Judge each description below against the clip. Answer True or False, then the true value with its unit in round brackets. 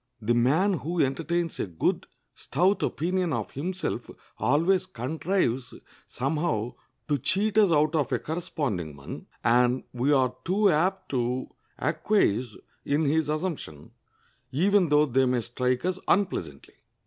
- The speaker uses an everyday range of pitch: False (6.3 semitones)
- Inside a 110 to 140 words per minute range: True (135 wpm)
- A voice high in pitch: False (150 Hz)